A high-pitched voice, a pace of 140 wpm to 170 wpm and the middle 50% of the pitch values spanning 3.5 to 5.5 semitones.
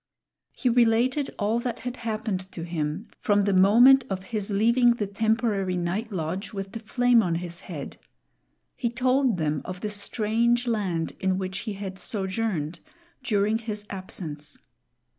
Yes: high, 205 Hz; average, 155 wpm; average, 3.8 semitones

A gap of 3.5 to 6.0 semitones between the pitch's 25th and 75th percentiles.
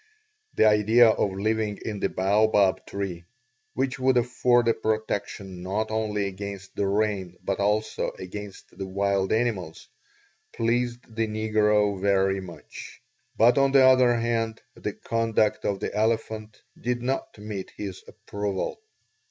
No: narrow, 2.5 semitones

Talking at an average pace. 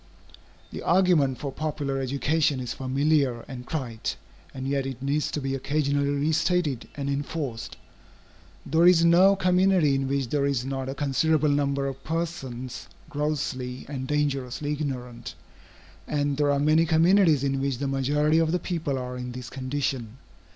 Yes: average, 160 wpm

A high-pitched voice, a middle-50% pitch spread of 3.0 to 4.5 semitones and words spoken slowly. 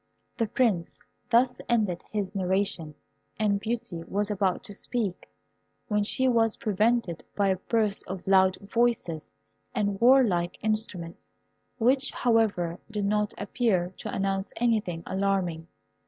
Yes: high, 205 Hz; average, 3.3 semitones; slow, 125 wpm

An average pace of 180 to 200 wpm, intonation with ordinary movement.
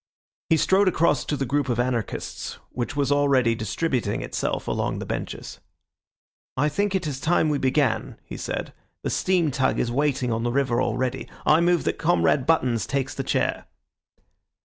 No: average, 170 wpm; average, 4.0 semitones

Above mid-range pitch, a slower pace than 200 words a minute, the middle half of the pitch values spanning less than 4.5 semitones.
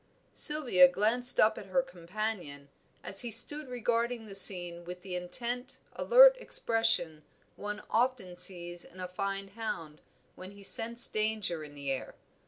No: high, 200 Hz; average, 150 wpm; average, 4.8 semitones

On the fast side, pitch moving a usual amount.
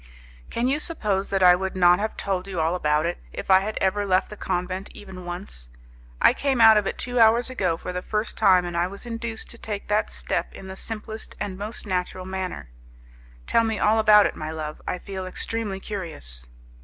Yes: fast, 215 wpm; average, 3.1 semitones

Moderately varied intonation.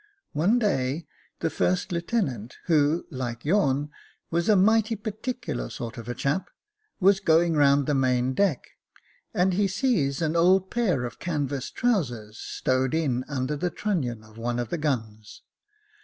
No: wide, 6.7 semitones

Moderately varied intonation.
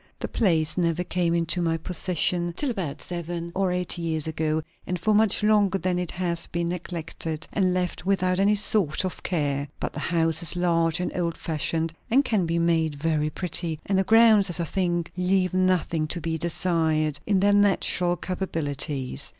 No: narrow, 2.3 semitones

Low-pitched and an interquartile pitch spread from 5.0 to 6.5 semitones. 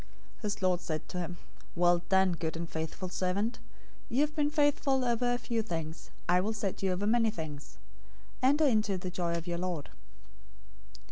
No: high, 190 Hz; average, 5.3 semitones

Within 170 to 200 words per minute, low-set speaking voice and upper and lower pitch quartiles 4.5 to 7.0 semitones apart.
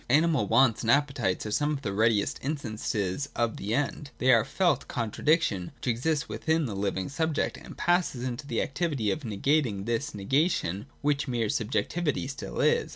Yes: average, 180 wpm; low, 130 Hz; wide, 5.4 semitones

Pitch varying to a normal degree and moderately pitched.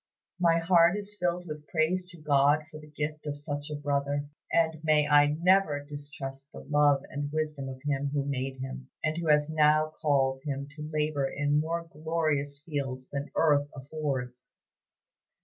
No: narrow, 1.8 semitones; medium, 150 Hz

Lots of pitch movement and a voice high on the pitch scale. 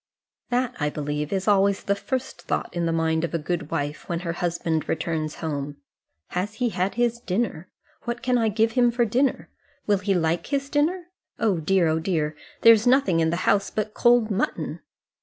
Yes: wide, 6.5 semitones; high, 195 Hz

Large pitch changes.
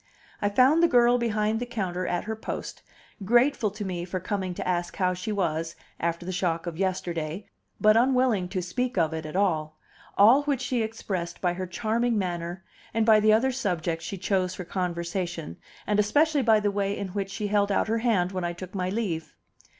No: average, 3.9 semitones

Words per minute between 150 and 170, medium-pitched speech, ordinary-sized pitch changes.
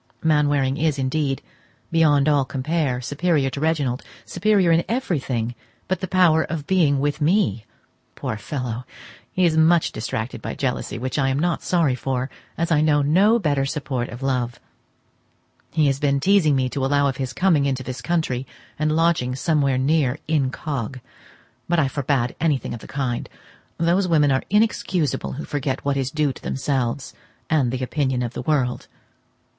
Yes: average, 165 wpm; medium, 145 Hz; average, 3.5 semitones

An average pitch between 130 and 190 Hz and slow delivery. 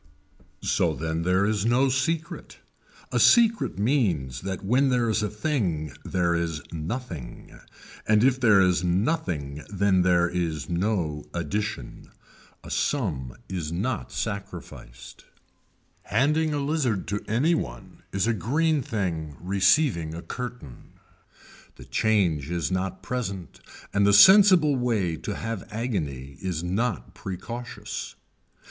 No: low, 100 Hz; slow, 125 wpm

